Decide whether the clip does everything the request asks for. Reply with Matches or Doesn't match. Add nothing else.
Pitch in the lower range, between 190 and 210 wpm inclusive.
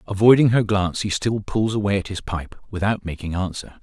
Matches